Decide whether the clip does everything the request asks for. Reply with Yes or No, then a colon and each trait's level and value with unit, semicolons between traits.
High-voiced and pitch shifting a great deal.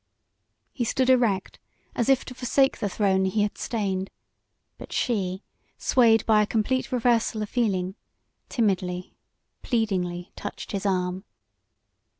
No: high, 210 Hz; average, 4.0 semitones